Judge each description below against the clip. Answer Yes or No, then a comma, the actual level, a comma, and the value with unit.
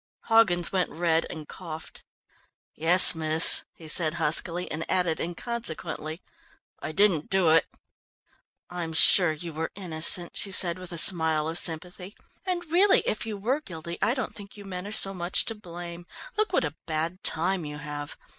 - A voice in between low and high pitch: Yes, medium, 175 Hz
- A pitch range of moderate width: Yes, average, 3.3 semitones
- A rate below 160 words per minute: No, average, 170 wpm